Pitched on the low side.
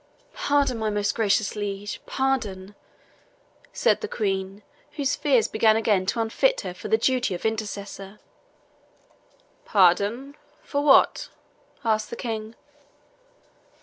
No: high, 220 Hz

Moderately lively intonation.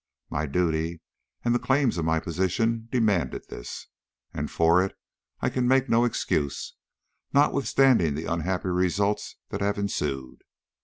No: wide, 6.3 semitones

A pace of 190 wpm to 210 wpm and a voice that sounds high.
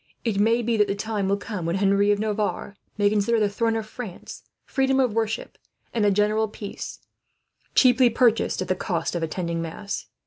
Yes: average, 195 wpm; high, 210 Hz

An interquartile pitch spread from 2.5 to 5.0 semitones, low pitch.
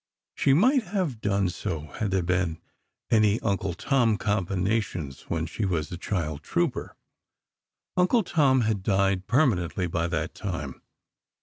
No: wide, 5.5 semitones; low, 100 Hz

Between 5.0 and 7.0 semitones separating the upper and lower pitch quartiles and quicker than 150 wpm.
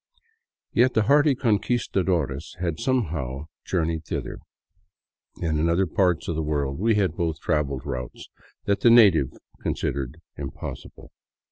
No: wide, 5.6 semitones; slow, 135 wpm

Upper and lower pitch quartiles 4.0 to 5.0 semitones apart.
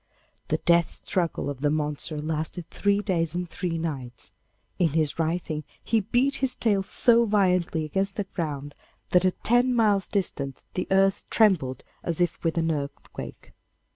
Yes: average, 4.3 semitones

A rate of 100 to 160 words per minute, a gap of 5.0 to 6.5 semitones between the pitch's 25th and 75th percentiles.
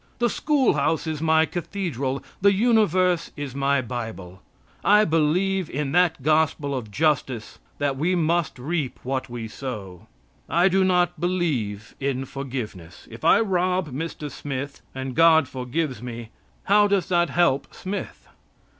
Yes: average, 145 wpm; wide, 5.5 semitones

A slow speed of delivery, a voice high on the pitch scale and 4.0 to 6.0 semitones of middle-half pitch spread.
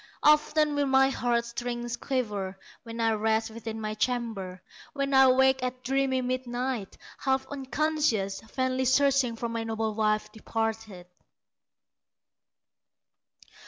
No: slow, 120 wpm; high, 240 Hz; average, 3.1 semitones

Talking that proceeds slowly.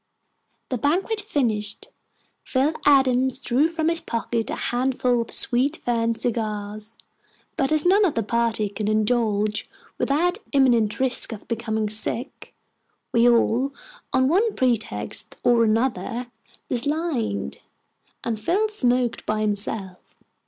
Yes: slow, 125 wpm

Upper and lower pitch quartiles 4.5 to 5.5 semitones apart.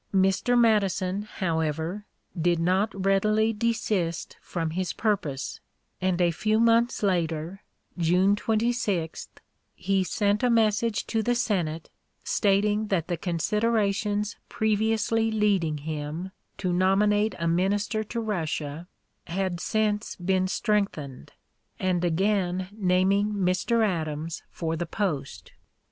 No: average, 3.7 semitones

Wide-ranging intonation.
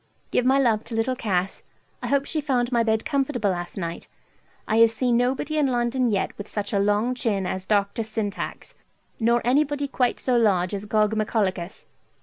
No: average, 3.7 semitones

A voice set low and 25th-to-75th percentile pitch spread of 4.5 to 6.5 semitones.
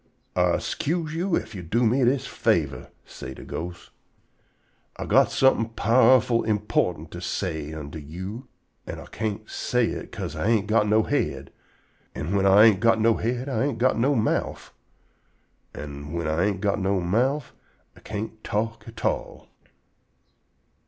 Yes: low, 110 Hz; average, 4.8 semitones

